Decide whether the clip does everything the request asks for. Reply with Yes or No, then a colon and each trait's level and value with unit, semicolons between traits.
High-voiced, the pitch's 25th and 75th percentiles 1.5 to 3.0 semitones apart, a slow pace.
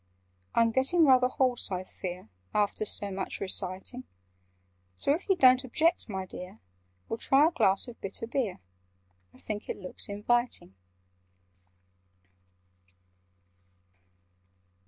No: high, 225 Hz; average, 5.3 semitones; slow, 115 wpm